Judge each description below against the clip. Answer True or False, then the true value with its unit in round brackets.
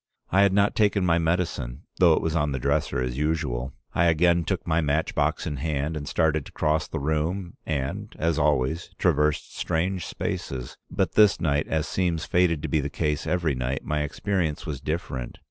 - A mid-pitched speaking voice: False (80 Hz)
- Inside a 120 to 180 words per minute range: False (195 wpm)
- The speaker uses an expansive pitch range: False (3.0 semitones)